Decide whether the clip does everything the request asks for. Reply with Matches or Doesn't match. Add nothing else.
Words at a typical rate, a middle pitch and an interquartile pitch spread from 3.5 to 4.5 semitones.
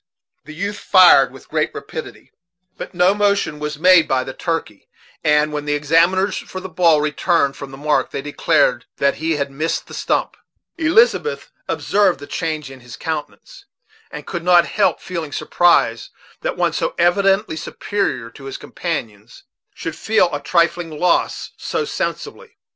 Matches